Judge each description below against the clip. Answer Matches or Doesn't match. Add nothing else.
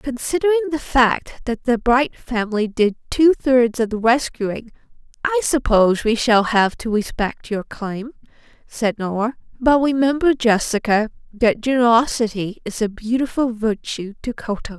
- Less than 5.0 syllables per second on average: Matches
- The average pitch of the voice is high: Matches